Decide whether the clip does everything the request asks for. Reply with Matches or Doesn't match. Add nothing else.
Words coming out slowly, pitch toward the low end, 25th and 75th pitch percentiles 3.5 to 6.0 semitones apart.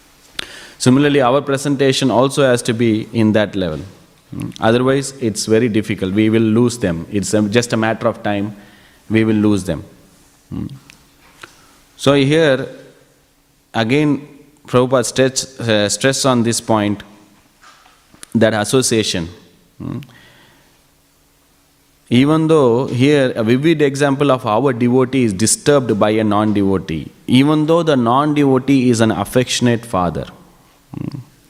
Matches